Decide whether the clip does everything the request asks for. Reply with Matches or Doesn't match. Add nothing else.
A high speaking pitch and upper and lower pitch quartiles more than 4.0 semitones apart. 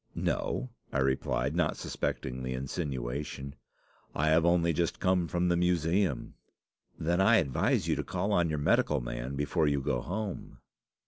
Doesn't match